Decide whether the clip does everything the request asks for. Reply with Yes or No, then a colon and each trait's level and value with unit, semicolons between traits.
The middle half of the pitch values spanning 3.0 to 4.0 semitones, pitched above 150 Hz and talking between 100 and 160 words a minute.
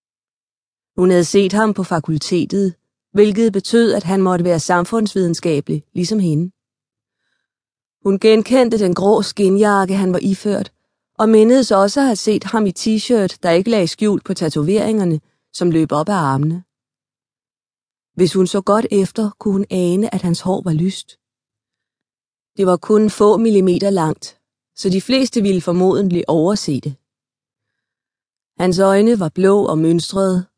Yes: average, 3.7 semitones; high, 190 Hz; slow, 145 wpm